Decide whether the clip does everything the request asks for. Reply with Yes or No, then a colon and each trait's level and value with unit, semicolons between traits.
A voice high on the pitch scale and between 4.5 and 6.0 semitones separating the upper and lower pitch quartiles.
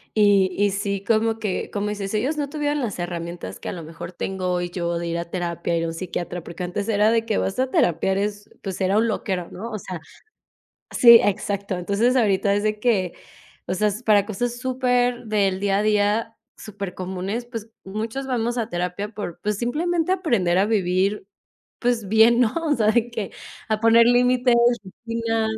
No: high, 210 Hz; average, 3.7 semitones